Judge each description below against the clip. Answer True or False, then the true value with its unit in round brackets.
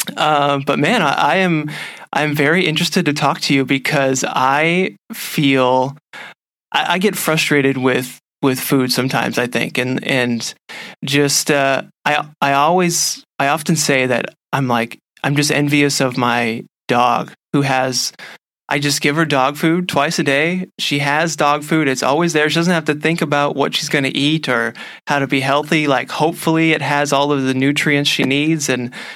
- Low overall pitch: False (145 Hz)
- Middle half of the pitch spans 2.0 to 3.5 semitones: True (2.8 semitones)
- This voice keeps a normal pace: True (185 wpm)